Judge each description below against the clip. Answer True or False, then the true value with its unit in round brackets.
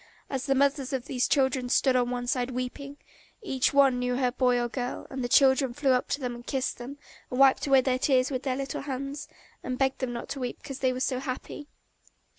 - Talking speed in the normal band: False (235 wpm)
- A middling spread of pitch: False (1.5 semitones)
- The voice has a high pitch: True (260 Hz)